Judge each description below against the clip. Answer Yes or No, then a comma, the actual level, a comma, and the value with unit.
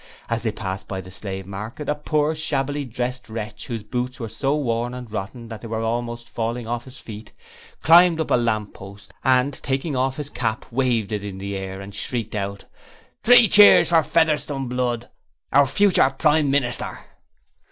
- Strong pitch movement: No, average, 4.6 semitones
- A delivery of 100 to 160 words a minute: No, average, 185 wpm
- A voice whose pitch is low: Yes, low, 120 Hz